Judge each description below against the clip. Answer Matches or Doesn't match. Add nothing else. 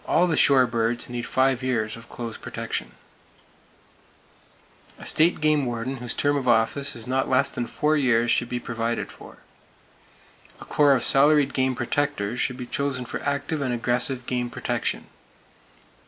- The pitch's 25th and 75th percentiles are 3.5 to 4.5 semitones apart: Doesn't match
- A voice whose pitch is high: Doesn't match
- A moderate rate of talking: Matches